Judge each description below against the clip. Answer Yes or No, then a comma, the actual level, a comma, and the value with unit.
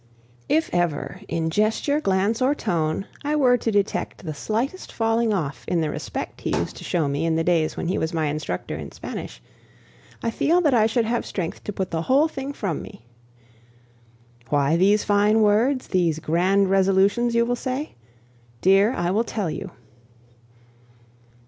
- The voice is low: No, high, 200 Hz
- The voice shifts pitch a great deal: Yes, wide, 5.8 semitones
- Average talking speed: Yes, average, 175 wpm